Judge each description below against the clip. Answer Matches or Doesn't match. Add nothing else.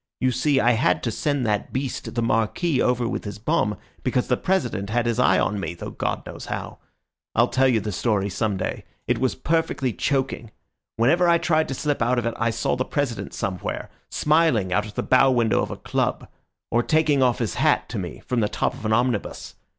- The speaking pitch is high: Doesn't match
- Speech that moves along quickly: Matches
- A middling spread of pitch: Matches